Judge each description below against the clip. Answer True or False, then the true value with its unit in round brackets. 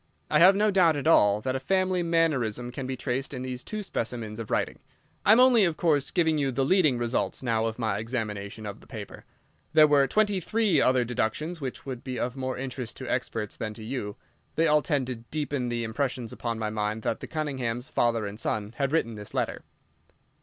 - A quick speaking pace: True (215 wpm)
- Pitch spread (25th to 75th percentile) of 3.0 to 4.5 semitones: False (5.3 semitones)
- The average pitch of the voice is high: False (130 Hz)